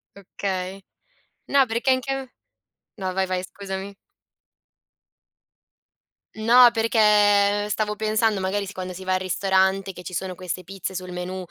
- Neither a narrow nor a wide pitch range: No, narrow, 2.3 semitones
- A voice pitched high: Yes, high, 195 Hz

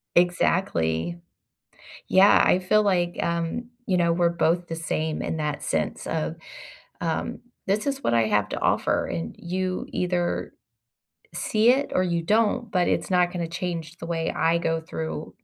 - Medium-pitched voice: Yes, medium, 175 Hz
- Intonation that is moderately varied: No, narrow, 2.2 semitones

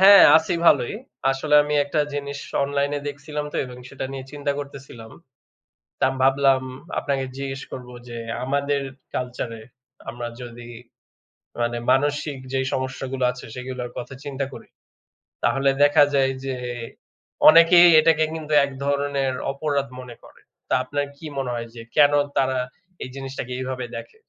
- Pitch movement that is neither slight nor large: No, narrow, 2.0 semitones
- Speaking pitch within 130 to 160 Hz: Yes, low, 135 Hz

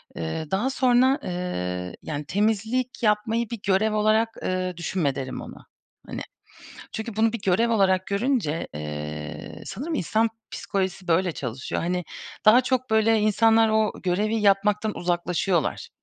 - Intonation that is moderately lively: Yes, average, 4.3 semitones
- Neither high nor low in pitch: No, high, 205 Hz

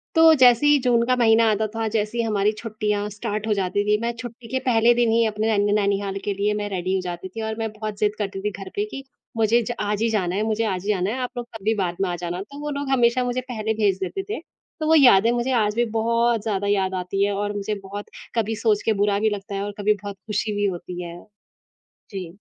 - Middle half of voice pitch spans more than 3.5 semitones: No, average, 2.7 semitones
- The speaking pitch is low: No, high, 210 Hz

